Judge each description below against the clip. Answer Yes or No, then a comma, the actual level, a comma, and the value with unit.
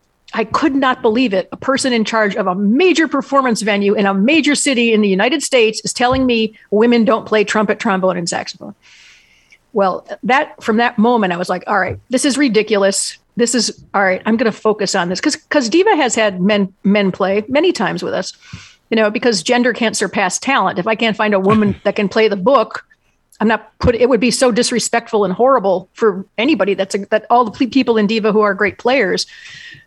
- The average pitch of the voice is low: No, high, 220 Hz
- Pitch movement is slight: No, average, 3.9 semitones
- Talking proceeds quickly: Yes, fast, 220 wpm